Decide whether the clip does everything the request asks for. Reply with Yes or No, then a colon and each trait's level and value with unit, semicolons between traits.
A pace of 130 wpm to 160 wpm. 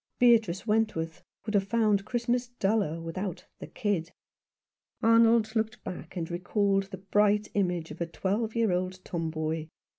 Yes: average, 145 wpm